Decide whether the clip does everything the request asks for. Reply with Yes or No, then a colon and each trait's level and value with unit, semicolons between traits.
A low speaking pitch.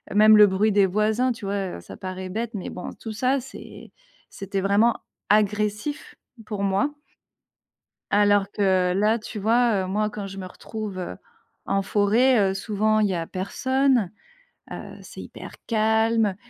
No: high, 210 Hz